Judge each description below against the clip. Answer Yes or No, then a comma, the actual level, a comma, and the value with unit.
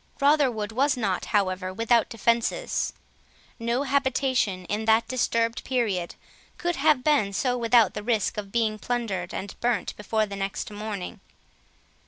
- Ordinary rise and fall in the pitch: Yes, average, 3.6 semitones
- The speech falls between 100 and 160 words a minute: Yes, average, 140 wpm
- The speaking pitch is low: No, high, 230 Hz